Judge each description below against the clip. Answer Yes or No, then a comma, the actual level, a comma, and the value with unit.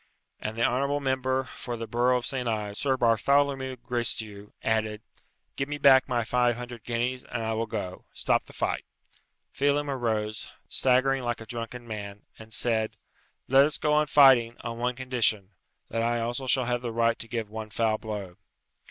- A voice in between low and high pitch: No, low, 120 Hz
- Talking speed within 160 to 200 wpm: Yes, average, 180 wpm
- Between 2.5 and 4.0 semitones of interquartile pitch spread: Yes, average, 2.8 semitones